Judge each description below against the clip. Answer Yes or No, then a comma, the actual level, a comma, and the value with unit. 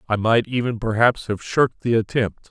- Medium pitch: No, low, 110 Hz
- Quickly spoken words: No, average, 190 wpm